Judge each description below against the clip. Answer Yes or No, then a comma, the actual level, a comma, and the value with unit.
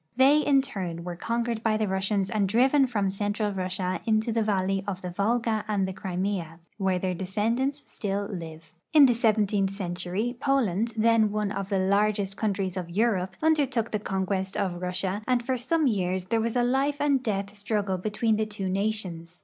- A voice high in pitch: Yes, high, 205 Hz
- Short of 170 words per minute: No, average, 185 wpm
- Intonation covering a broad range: No, average, 3.5 semitones